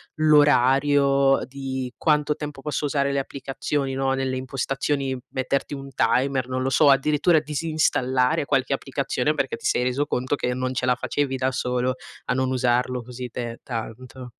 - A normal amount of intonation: No, narrow, 2.0 semitones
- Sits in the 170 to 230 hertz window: No, low, 135 Hz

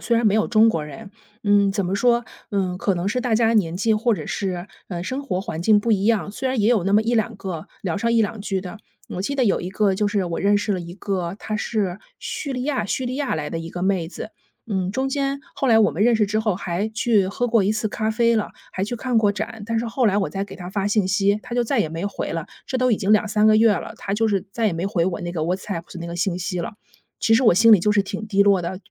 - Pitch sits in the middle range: No, high, 205 Hz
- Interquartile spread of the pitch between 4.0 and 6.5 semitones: No, average, 3.2 semitones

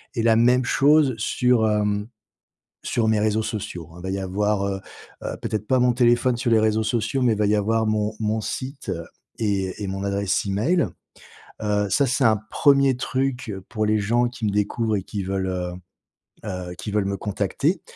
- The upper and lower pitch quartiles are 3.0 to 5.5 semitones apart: Yes, average, 3.3 semitones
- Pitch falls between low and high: No, low, 110 Hz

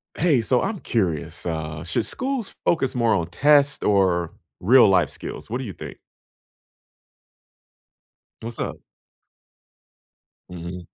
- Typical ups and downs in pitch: No, wide, 7.8 semitones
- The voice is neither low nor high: No, low, 105 Hz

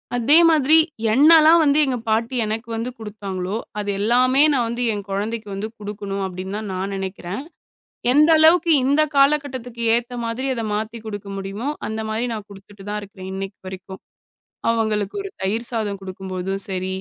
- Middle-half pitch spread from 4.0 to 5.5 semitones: Yes, average, 4.3 semitones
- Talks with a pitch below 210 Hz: No, high, 220 Hz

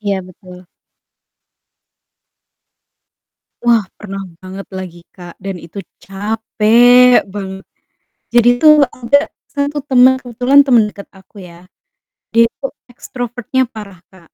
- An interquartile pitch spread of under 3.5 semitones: No, average, 4.4 semitones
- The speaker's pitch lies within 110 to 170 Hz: No, high, 215 Hz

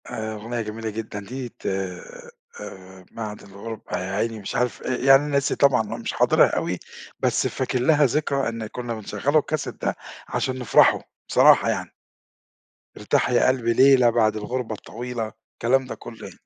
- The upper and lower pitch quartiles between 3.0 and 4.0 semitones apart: Yes, average, 3.5 semitones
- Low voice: Yes, low, 120 Hz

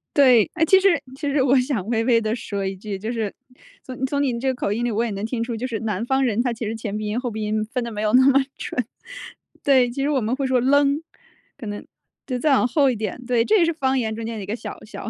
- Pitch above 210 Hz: Yes, high, 240 Hz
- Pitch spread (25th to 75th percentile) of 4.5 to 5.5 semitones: No, average, 3.5 semitones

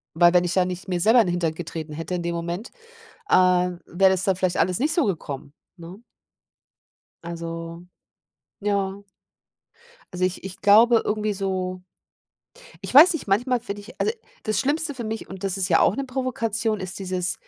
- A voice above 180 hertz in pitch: Yes, high, 190 Hz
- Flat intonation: No, average, 3.7 semitones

